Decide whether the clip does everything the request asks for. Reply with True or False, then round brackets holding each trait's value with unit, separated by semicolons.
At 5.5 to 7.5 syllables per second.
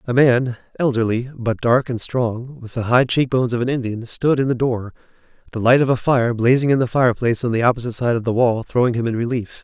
True (6.0 syllables/s)